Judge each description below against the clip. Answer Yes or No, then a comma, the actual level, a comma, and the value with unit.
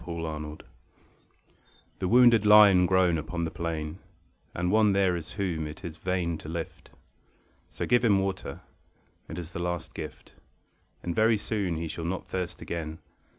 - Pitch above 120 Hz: No, very low, 85 Hz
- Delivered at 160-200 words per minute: Yes, average, 165 wpm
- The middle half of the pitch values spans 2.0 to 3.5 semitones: Yes, average, 3.1 semitones